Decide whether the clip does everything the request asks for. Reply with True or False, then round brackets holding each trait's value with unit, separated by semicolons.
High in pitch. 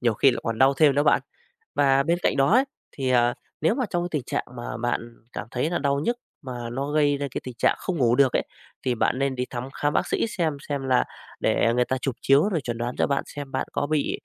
False (135 Hz)